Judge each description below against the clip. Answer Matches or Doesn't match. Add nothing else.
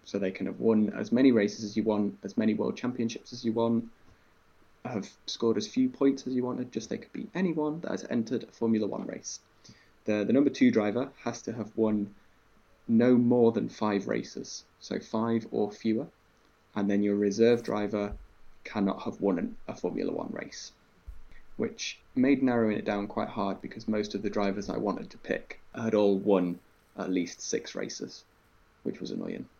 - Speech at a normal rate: Matches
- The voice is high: Doesn't match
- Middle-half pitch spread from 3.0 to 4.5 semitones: Doesn't match